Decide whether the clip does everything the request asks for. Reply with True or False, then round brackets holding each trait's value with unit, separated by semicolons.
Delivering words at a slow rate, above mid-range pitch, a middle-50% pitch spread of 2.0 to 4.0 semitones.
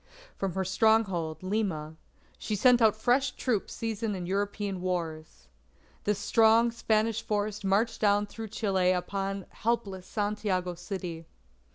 True (130 wpm; 205 Hz; 3.1 semitones)